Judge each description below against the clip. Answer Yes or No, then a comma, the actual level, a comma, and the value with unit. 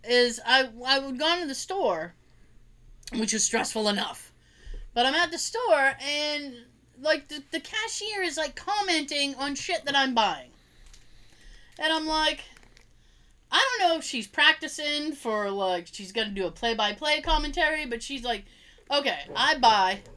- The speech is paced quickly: No, average, 165 wpm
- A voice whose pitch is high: Yes, very high, 285 Hz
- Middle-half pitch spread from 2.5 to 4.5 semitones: No, average, 5.1 semitones